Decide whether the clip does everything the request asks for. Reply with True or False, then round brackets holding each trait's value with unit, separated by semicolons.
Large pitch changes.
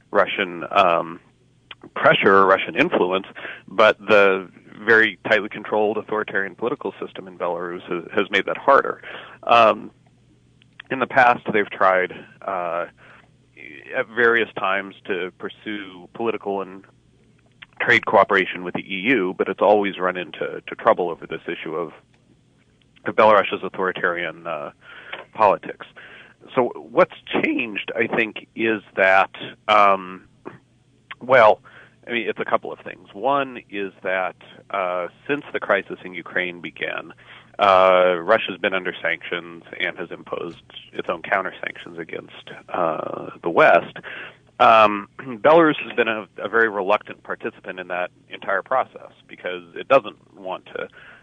False (3.5 semitones)